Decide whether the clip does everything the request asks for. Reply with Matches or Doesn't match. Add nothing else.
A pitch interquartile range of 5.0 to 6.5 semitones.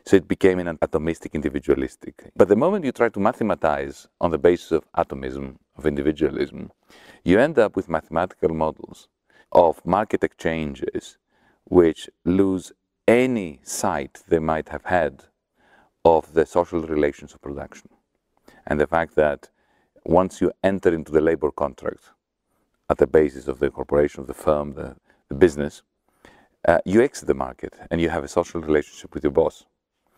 Doesn't match